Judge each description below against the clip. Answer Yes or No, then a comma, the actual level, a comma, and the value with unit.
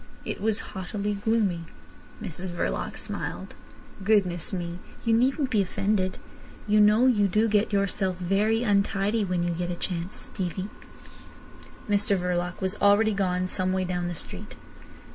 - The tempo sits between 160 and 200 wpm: No, average, 145 wpm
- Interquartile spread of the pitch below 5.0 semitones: Yes, average, 2.8 semitones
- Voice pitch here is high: Yes, high, 195 Hz